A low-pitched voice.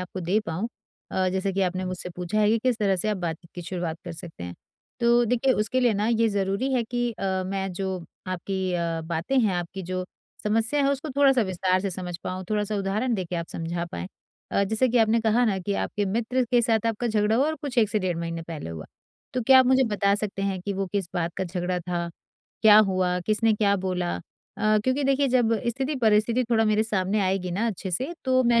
No: high, 200 Hz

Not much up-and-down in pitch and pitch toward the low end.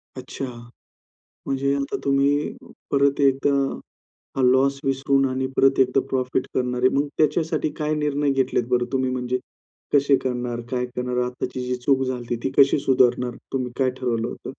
Yes: narrow, 1.6 semitones; low, 130 Hz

